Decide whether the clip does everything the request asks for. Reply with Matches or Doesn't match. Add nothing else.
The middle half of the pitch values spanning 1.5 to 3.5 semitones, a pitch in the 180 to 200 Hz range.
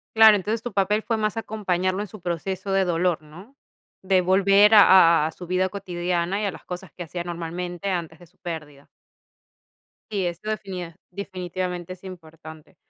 Matches